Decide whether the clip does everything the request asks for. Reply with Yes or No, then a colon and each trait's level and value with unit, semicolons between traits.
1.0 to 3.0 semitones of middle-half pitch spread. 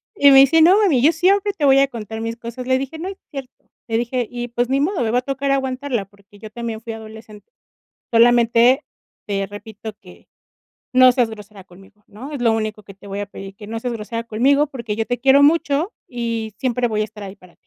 No: average, 3.9 semitones